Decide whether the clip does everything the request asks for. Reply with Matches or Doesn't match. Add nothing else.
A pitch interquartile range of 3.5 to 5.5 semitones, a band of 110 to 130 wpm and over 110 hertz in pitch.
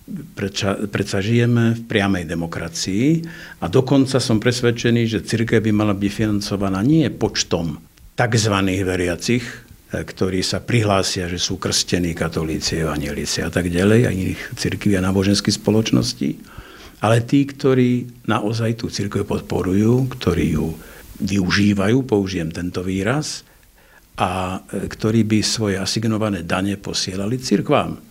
Doesn't match